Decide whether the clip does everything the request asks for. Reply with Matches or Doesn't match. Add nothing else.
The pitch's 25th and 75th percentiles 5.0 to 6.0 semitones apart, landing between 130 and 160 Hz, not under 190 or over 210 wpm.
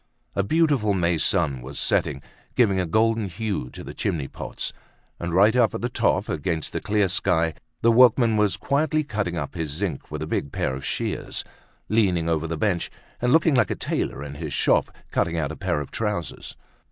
Doesn't match